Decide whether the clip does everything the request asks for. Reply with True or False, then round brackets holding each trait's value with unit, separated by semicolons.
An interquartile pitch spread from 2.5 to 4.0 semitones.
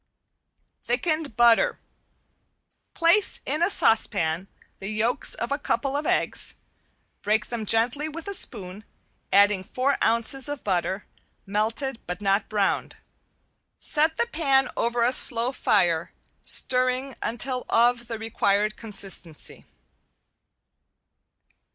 False (4.7 semitones)